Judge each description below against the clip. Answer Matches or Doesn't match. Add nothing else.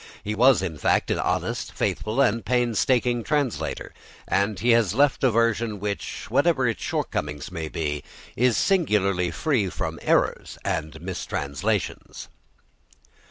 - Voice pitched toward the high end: Doesn't match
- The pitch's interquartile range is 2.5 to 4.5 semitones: Doesn't match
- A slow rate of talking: Matches